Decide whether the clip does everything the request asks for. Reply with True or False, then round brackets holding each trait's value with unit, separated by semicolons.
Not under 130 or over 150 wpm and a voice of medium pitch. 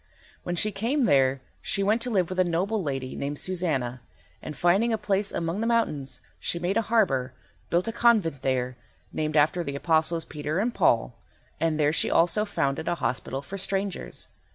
False (185 wpm; 170 Hz)